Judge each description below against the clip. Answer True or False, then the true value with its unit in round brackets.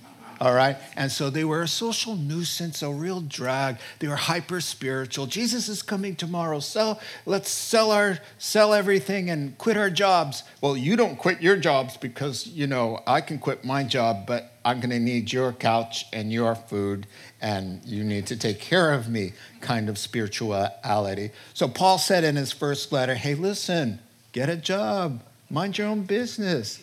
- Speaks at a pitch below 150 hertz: True (140 Hz)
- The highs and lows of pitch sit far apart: True (7.7 semitones)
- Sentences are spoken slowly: False (180 wpm)